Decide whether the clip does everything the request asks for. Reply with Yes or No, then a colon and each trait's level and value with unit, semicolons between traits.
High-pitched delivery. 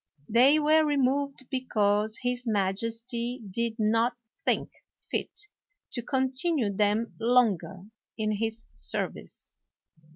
Yes: high, 235 Hz